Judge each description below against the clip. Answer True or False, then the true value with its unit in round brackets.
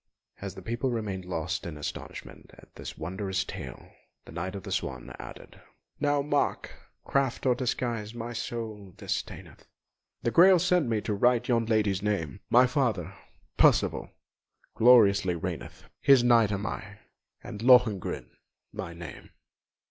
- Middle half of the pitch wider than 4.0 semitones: True (4.5 semitones)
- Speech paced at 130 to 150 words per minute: True (140 wpm)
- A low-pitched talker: True (110 Hz)